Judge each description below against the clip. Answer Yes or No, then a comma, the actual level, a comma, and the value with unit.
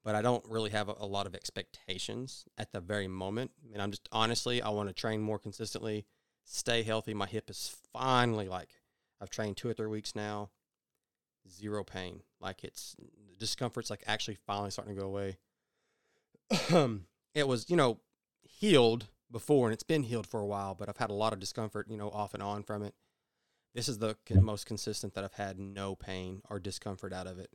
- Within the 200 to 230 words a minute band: Yes, fast, 205 wpm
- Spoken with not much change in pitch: Yes, narrow, 2.3 semitones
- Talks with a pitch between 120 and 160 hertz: No, low, 105 Hz